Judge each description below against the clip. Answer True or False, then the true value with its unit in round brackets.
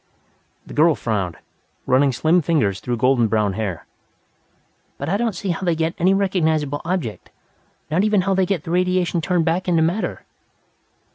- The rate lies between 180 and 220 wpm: False (165 wpm)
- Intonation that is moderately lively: False (6.0 semitones)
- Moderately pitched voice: True (165 Hz)